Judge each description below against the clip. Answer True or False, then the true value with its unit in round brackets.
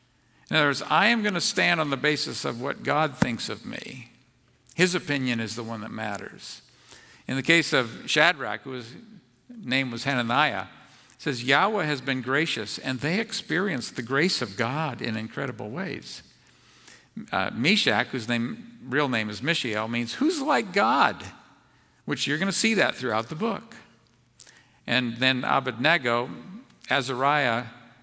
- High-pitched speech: False (130 Hz)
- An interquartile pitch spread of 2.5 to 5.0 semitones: False (5.6 semitones)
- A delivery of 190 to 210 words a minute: False (155 wpm)